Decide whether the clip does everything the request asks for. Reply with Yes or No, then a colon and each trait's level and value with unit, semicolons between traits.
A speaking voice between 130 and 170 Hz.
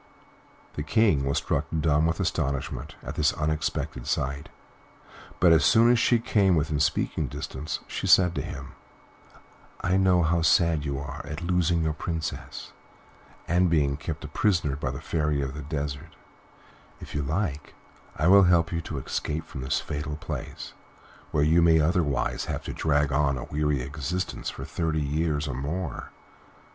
No: very low, 75 Hz